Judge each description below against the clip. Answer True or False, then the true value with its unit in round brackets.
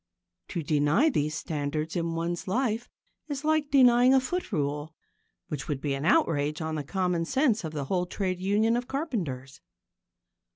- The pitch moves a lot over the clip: True (8.3 semitones)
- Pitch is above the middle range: False (175 Hz)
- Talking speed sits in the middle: True (165 wpm)